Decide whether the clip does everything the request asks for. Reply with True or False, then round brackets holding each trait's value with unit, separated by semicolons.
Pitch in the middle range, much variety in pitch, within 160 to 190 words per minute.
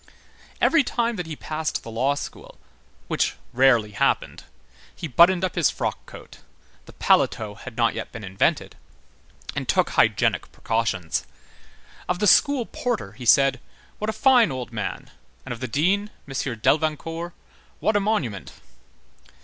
False (145 Hz; 8.8 semitones; 140 wpm)